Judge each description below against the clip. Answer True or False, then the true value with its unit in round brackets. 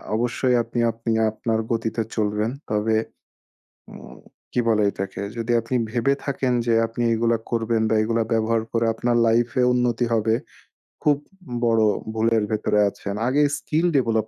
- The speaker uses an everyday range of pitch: False (1.5 semitones)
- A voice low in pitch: True (115 Hz)